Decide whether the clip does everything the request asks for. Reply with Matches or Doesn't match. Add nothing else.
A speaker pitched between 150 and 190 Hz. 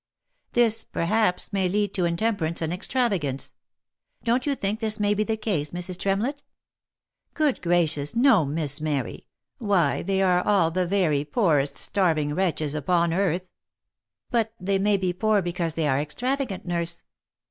Matches